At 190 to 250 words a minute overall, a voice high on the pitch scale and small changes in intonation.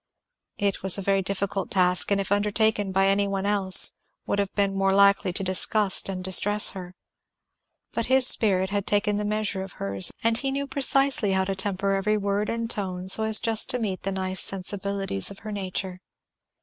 Yes: average, 195 wpm; high, 200 Hz; narrow, 1.7 semitones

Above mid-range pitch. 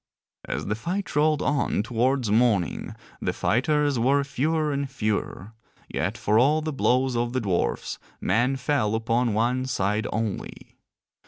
No: low, 125 Hz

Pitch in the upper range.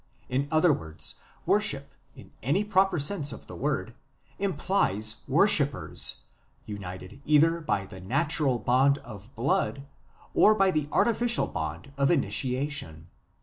No: medium, 140 Hz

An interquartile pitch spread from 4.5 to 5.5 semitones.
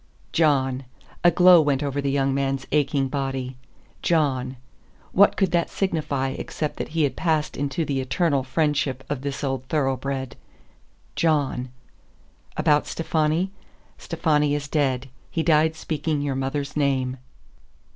No: average, 2.7 semitones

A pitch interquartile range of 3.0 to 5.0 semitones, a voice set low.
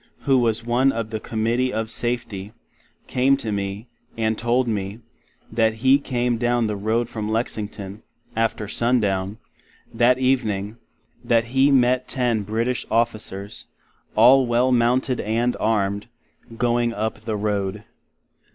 No: narrow, 2.4 semitones; low, 115 Hz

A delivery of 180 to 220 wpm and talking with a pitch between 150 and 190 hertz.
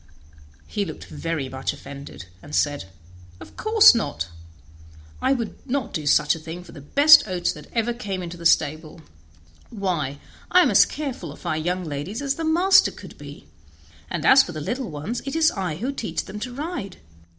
Yes: average, 190 wpm; medium, 185 Hz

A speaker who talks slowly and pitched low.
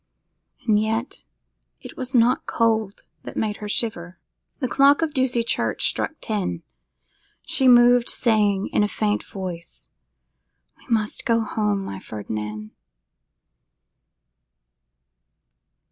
No: slow, 115 wpm; high, 215 Hz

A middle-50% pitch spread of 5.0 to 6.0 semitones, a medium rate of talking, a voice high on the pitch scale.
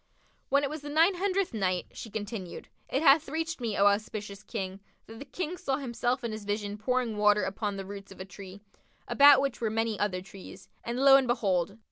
No: average, 5.3 semitones; fast, 210 wpm; high, 225 Hz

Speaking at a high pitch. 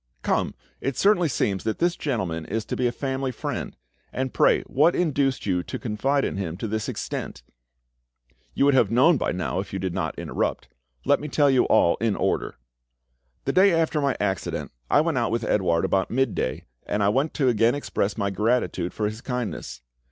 No: low, 120 Hz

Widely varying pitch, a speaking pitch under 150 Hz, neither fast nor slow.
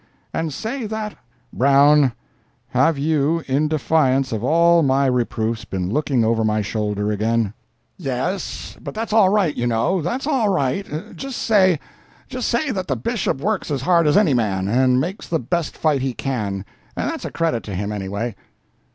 Yes: wide, 7.3 semitones; medium, 140 Hz; average, 165 wpm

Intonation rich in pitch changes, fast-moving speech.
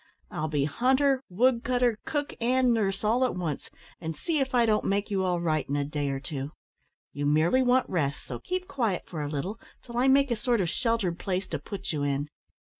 Yes: wide, 8.3 semitones; fast, 215 wpm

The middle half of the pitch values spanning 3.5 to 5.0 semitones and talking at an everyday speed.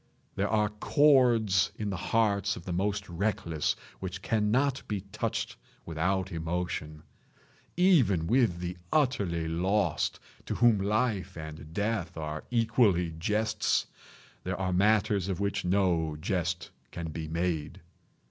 No: average, 4.1 semitones; slow, 130 wpm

